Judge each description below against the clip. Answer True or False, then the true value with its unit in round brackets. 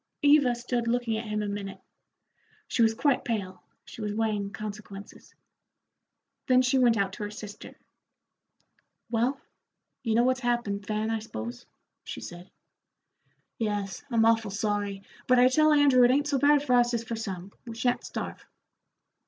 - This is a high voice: True (225 Hz)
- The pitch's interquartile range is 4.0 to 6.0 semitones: False (3.3 semitones)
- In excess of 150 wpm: True (160 wpm)